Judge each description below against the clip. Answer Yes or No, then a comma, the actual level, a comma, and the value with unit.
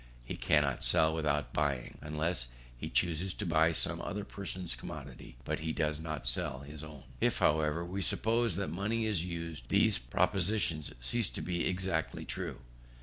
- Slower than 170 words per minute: Yes, average, 160 wpm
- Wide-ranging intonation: No, average, 3.6 semitones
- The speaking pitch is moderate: No, very low, 80 Hz